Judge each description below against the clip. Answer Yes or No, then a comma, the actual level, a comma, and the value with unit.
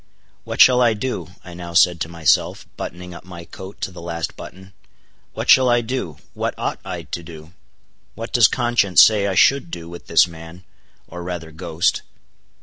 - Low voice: Yes, very low, 90 Hz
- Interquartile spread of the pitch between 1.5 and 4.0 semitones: No, average, 4.6 semitones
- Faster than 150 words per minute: Yes, average, 185 wpm